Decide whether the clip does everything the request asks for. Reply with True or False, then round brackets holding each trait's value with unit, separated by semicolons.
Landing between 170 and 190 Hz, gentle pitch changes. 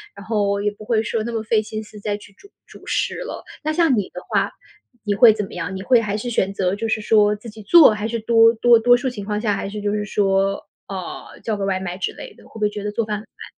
False (210 Hz; 2.1 semitones)